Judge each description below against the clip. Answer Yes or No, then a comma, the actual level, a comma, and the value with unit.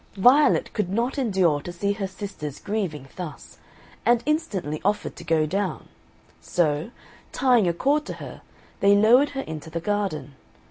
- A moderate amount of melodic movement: No, wide, 5.9 semitones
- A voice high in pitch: Yes, high, 200 Hz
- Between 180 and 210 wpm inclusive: No, average, 155 wpm